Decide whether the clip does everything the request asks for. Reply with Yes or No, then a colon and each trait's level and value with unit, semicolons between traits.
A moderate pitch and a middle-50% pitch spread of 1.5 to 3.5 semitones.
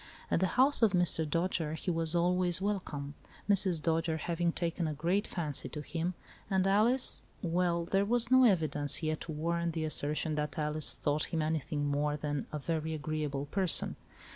Yes: medium, 165 Hz; average, 3.1 semitones